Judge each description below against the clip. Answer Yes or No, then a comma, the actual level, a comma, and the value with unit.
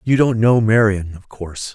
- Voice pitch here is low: Yes, low, 110 Hz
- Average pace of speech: Yes, average, 170 wpm